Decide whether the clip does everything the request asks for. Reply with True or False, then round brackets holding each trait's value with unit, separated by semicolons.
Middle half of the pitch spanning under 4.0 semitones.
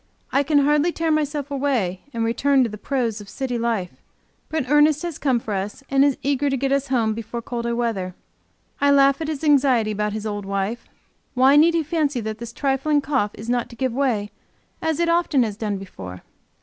False (4.6 semitones)